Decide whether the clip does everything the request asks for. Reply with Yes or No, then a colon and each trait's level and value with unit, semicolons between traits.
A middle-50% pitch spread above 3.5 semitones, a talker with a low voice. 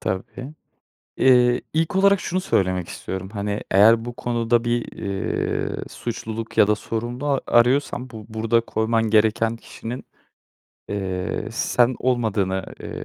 No: average, 2.8 semitones; low, 115 Hz